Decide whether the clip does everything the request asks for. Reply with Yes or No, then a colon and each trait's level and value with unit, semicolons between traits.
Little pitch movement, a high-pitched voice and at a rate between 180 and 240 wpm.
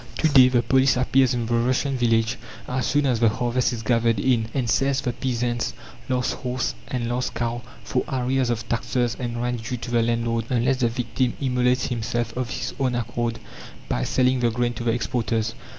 No: narrow, 1.6 semitones; low, 120 Hz; average, 200 wpm